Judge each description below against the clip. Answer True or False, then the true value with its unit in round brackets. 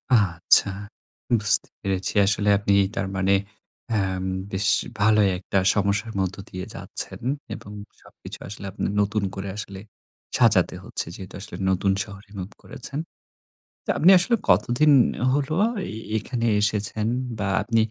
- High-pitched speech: False (100 Hz)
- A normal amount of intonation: False (2.3 semitones)